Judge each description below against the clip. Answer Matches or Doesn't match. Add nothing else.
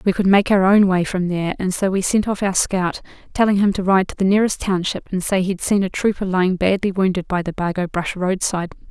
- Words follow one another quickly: Matches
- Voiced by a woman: Matches